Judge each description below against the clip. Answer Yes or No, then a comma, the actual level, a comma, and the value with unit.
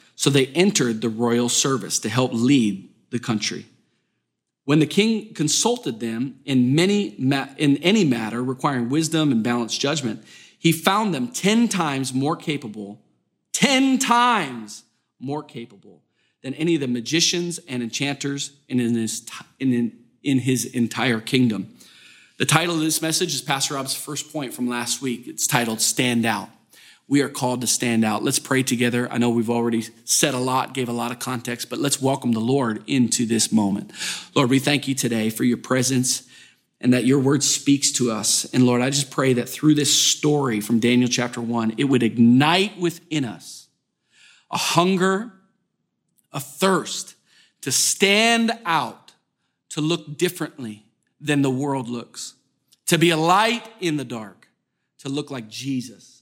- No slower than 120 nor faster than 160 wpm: No, average, 170 wpm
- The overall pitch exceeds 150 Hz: No, low, 135 Hz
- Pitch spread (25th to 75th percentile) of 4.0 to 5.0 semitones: Yes, average, 4.3 semitones